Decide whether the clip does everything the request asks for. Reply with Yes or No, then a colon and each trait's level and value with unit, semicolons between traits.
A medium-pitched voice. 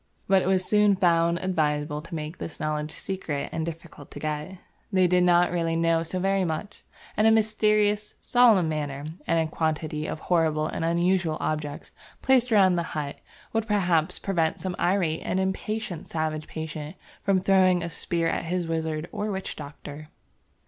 Yes: medium, 170 Hz